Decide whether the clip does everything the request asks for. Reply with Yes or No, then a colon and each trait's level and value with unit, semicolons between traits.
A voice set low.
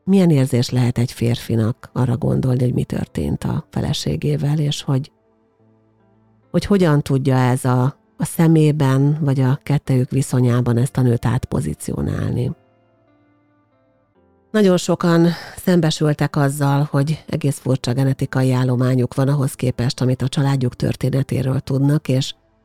Yes: low, 130 Hz